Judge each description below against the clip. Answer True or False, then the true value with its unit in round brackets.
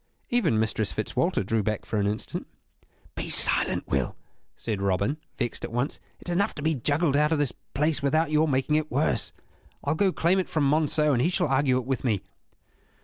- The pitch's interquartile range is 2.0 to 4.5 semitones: False (5.6 semitones)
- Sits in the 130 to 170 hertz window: True (140 Hz)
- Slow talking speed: False (205 wpm)